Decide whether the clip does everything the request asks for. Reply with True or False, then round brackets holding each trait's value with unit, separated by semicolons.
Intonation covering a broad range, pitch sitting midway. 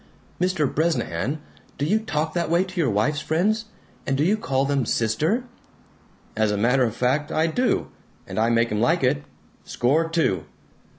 True (6.2 semitones; 150 Hz)